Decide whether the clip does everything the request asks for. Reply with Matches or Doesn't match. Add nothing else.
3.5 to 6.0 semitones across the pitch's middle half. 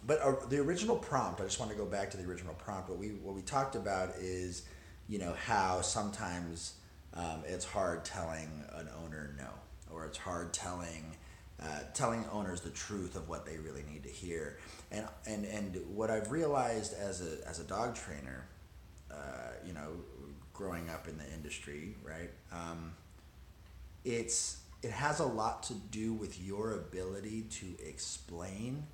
Matches